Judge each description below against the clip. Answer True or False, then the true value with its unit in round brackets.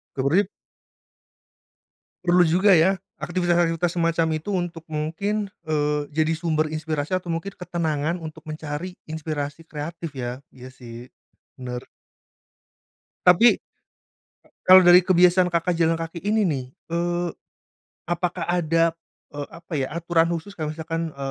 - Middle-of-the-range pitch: True (165 Hz)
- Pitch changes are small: True (2.3 semitones)